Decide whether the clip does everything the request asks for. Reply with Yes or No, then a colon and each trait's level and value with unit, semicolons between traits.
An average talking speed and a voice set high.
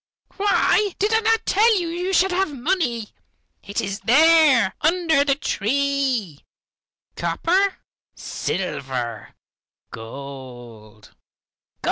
No: slow, 95 wpm; very high, 280 Hz